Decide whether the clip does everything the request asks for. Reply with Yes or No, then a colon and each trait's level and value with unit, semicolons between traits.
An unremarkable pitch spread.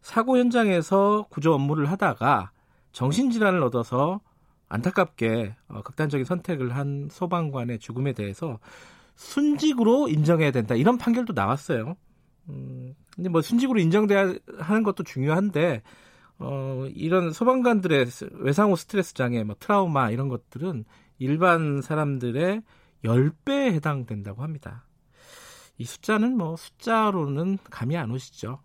No: wide, 7.1 semitones